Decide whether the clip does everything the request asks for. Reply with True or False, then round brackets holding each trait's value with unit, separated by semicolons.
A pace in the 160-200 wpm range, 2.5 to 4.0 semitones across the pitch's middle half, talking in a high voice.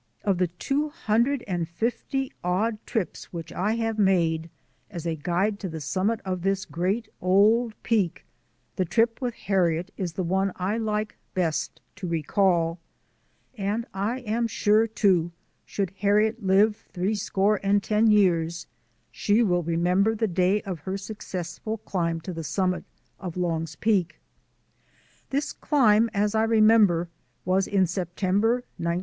False (145 wpm; 3.6 semitones; 195 Hz)